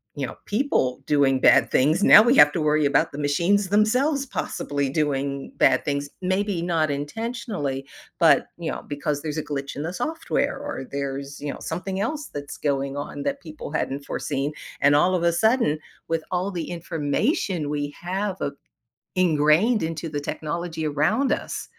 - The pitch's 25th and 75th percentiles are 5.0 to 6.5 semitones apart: Yes, average, 5.3 semitones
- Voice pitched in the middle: Yes, medium, 155 Hz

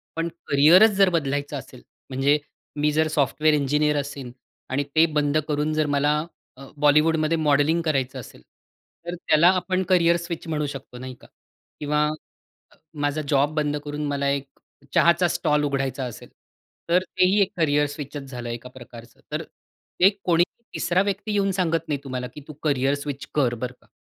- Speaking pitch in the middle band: Yes, medium, 150 Hz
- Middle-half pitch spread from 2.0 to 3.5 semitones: Yes, average, 3.1 semitones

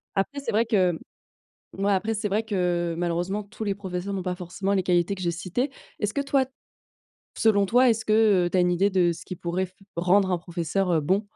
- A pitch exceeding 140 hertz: Yes, high, 190 Hz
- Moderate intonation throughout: Yes, average, 3.0 semitones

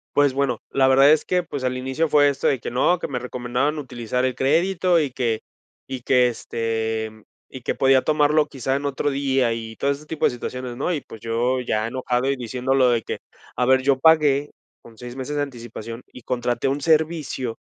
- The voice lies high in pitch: No, low, 130 Hz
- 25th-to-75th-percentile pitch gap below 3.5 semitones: Yes, average, 2.8 semitones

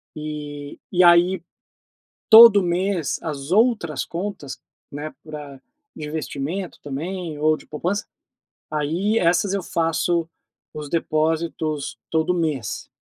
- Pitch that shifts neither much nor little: Yes, average, 3.2 semitones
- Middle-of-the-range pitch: Yes, medium, 165 Hz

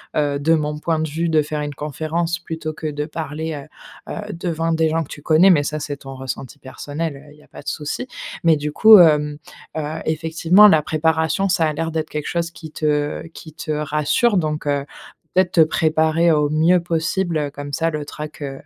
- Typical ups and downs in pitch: No, narrow, 1.8 semitones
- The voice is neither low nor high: Yes, medium, 155 Hz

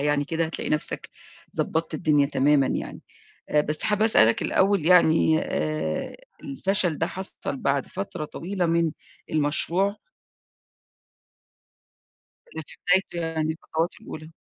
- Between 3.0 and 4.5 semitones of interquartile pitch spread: Yes, average, 3.5 semitones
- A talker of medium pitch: Yes, medium, 160 Hz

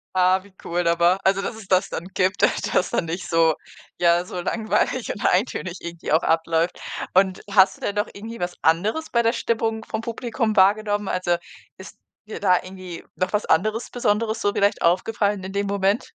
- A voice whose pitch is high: Yes, high, 195 Hz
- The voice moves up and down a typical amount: Yes, average, 3.3 semitones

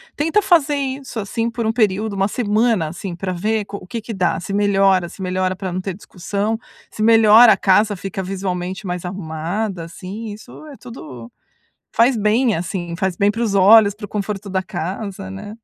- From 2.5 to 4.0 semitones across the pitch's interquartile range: Yes, average, 3.0 semitones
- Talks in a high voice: Yes, high, 200 Hz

